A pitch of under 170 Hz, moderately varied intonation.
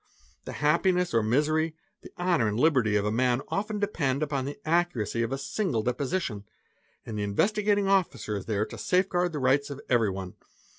No: medium, 140 Hz; wide, 7.6 semitones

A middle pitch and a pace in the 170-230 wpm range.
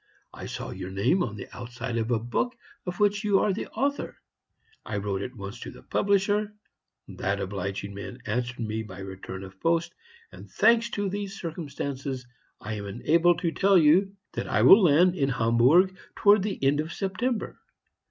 Yes: medium, 145 Hz; average, 180 wpm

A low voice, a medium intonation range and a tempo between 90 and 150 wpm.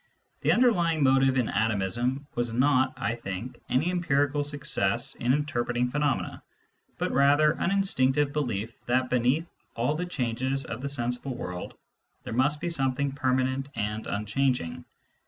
Yes: low, 130 Hz; average, 3.2 semitones; average, 145 wpm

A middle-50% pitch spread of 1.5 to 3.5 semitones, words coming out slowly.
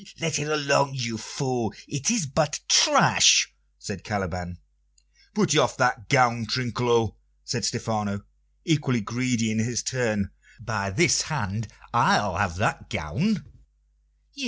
No: average, 4.6 semitones; slow, 125 wpm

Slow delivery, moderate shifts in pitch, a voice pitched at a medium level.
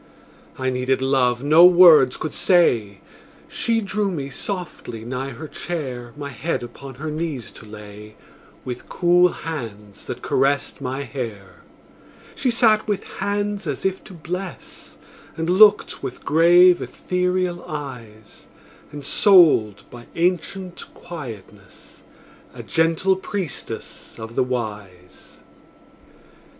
No: slow, 115 wpm; wide, 6.8 semitones; medium, 145 Hz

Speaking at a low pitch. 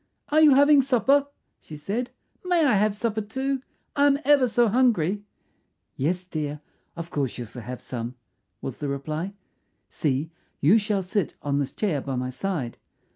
No: high, 195 Hz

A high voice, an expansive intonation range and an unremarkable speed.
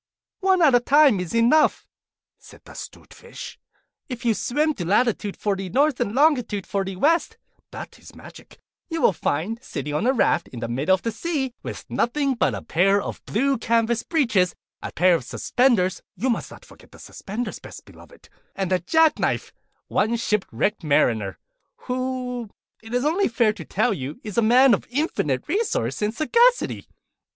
Yes: high, 230 Hz; wide, 6.2 semitones; average, 180 wpm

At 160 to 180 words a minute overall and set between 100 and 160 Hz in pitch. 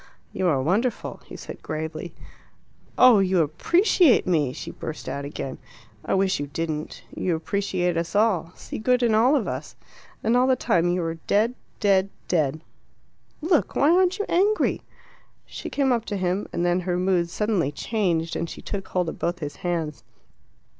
No: average, 175 wpm; medium, 185 Hz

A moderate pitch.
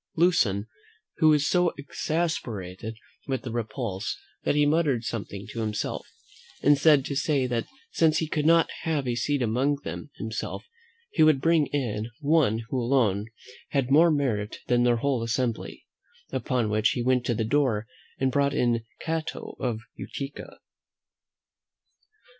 No: low, 130 Hz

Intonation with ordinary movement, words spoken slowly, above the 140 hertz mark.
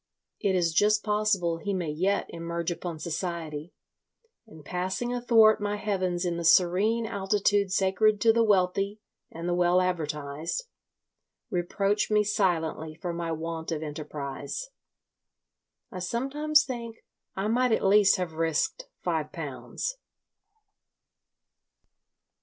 Yes: average, 4.1 semitones; slow, 125 wpm; medium, 185 Hz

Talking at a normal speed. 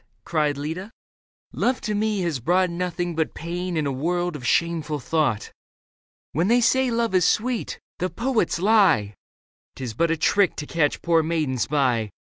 Yes: average, 170 wpm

